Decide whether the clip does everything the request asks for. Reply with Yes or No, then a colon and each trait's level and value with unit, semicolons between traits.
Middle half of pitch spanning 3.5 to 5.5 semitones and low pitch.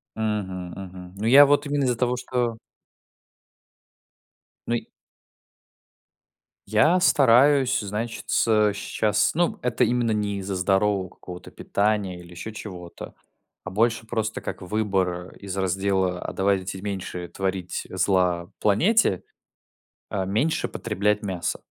Yes: average, 3.8 semitones; low, 100 Hz